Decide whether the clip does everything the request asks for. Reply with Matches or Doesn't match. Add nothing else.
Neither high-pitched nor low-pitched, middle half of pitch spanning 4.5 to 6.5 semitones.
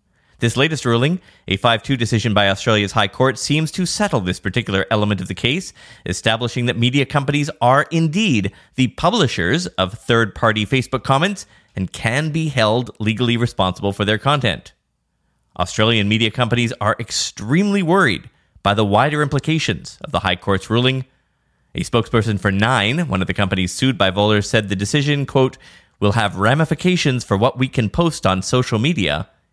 Doesn't match